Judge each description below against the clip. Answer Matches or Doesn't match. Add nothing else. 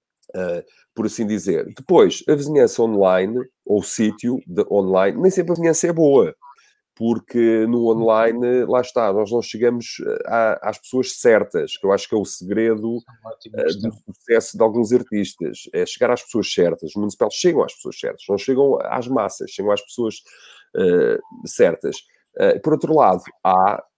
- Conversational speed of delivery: Matches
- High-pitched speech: Doesn't match